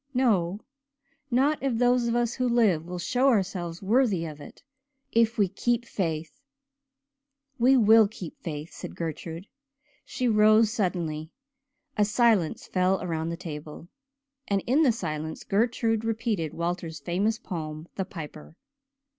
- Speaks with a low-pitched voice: No, high, 195 Hz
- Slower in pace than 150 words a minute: Yes, average, 140 wpm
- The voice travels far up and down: Yes, wide, 5.8 semitones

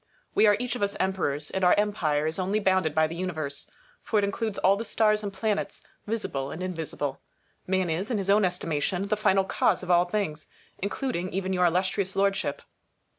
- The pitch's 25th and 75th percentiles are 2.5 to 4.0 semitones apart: Yes, average, 3.2 semitones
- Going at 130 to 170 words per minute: No, average, 195 wpm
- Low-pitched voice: No, high, 190 Hz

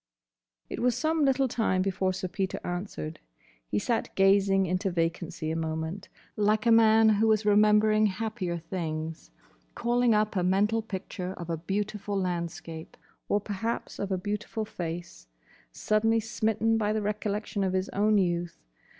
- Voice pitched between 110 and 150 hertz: No, high, 200 Hz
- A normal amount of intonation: Yes, average, 3.5 semitones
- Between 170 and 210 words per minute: No, average, 145 wpm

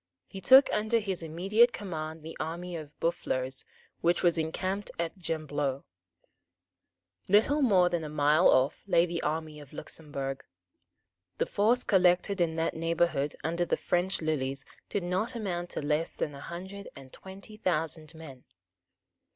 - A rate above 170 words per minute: No, average, 150 wpm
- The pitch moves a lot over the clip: No, average, 3.7 semitones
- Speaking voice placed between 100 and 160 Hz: No, medium, 170 Hz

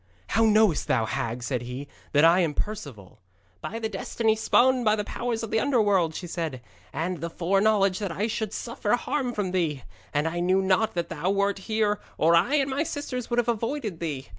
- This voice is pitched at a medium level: No, high, 200 Hz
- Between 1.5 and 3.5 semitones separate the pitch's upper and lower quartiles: No, average, 5.2 semitones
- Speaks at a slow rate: No, fast, 205 wpm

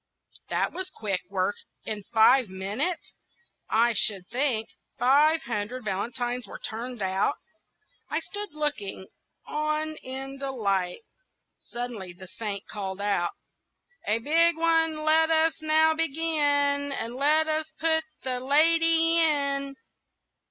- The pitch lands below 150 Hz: No, very high, 270 Hz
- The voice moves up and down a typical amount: No, wide, 6.4 semitones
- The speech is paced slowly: Yes, slow, 120 wpm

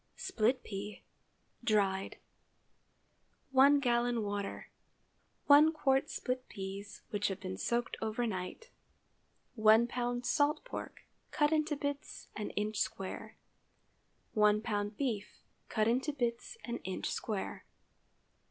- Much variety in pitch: No, average, 4.5 semitones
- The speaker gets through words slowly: Yes, slow, 115 wpm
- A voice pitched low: No, high, 235 Hz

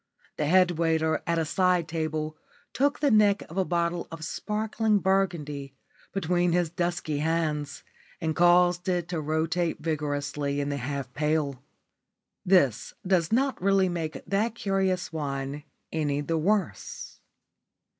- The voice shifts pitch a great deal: No, average, 3.4 semitones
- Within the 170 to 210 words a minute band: No, slow, 135 wpm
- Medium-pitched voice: Yes, medium, 165 Hz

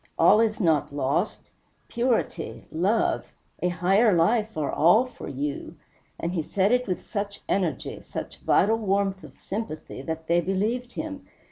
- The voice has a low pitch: No, high, 195 Hz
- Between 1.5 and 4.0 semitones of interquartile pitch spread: No, average, 5.1 semitones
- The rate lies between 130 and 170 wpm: Yes, average, 150 wpm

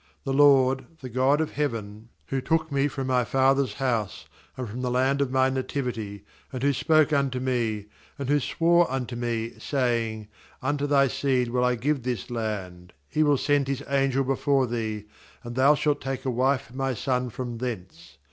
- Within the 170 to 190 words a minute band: Yes, average, 185 wpm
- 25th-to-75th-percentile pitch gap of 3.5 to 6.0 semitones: No, narrow, 2.6 semitones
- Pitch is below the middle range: Yes, low, 130 Hz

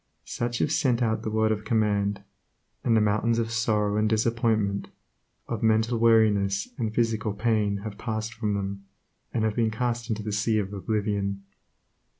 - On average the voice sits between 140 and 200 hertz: No, low, 110 Hz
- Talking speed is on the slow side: No, average, 165 wpm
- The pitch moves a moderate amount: No, narrow, 1.9 semitones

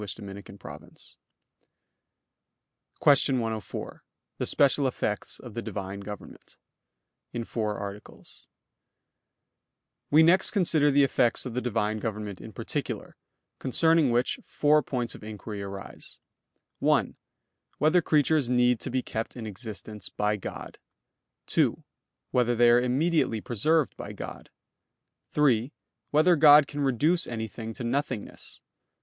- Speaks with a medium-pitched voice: No, low, 120 Hz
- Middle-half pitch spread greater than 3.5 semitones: Yes, average, 5.3 semitones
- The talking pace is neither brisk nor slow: No, slow, 120 wpm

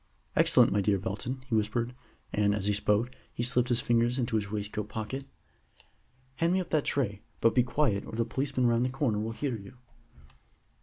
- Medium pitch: No, low, 115 Hz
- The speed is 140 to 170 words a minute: No, average, 195 wpm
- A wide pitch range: No, average, 3.4 semitones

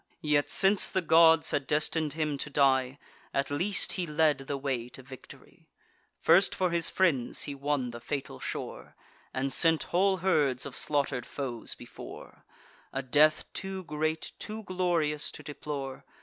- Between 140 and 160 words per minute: Yes, average, 155 wpm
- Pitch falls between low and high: Yes, medium, 150 Hz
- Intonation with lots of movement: No, average, 3.5 semitones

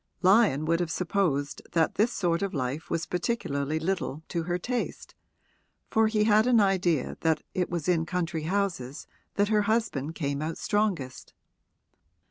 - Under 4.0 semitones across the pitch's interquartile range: No, average, 4.6 semitones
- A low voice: No, medium, 175 Hz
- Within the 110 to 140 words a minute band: No, average, 155 wpm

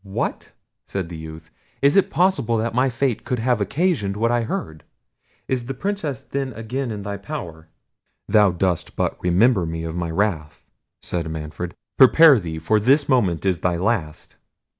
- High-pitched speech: No, low, 105 Hz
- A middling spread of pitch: No, wide, 7.2 semitones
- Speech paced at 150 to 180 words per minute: Yes, average, 170 wpm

